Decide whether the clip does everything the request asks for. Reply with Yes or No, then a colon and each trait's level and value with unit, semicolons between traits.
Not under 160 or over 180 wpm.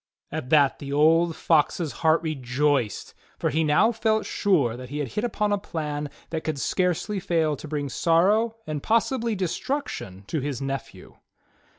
Yes: average, 165 wpm